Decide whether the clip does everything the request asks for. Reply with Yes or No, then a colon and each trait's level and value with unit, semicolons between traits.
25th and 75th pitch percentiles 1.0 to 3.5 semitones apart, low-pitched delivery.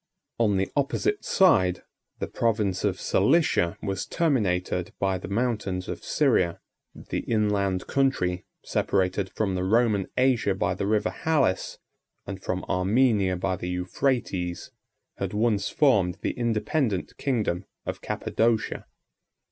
No: average, 4.4 semitones; low, 100 Hz